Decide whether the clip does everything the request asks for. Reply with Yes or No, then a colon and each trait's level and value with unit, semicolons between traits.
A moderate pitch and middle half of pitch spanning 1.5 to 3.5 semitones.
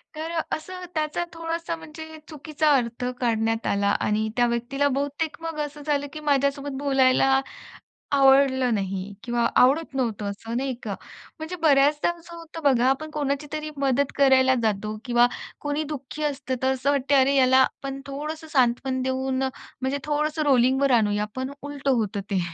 No: very high, 275 Hz; average, 3.2 semitones